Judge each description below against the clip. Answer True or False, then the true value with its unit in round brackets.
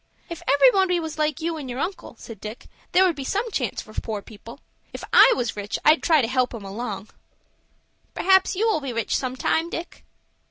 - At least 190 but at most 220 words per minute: True (200 wpm)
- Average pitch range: False (6.7 semitones)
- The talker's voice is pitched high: True (280 Hz)